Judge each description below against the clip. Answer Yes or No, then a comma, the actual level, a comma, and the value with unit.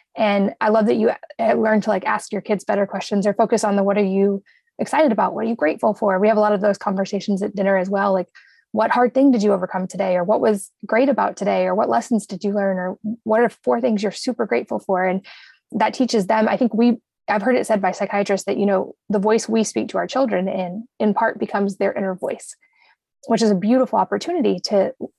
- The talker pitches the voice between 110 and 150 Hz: No, high, 210 Hz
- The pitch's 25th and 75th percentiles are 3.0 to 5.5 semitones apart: No, narrow, 2.4 semitones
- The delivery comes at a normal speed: No, fast, 245 wpm